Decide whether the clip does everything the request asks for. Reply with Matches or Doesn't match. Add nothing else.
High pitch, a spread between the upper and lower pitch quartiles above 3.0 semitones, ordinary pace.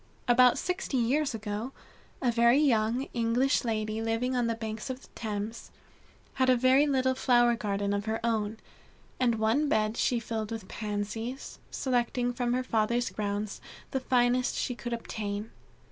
Doesn't match